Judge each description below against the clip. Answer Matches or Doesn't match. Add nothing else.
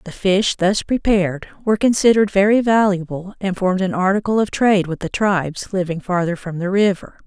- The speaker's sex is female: Matches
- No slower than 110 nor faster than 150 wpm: Doesn't match